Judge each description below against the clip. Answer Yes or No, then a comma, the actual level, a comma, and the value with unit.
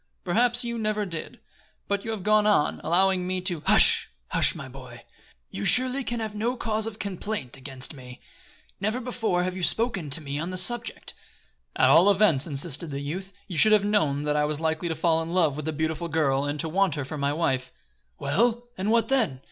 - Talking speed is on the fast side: Yes, fast, 215 wpm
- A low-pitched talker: No, medium, 180 Hz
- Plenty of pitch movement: Yes, wide, 6.3 semitones